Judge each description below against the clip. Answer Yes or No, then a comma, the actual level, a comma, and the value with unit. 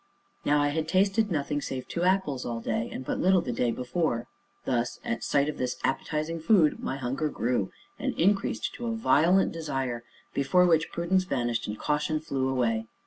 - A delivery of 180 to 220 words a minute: Yes, average, 185 wpm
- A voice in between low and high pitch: Yes, medium, 150 Hz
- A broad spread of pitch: Yes, wide, 5.9 semitones